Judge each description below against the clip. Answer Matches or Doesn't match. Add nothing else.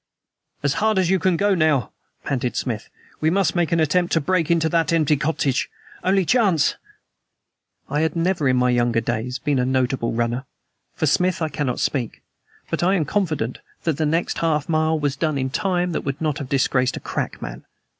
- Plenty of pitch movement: Doesn't match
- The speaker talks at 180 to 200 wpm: Matches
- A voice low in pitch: Doesn't match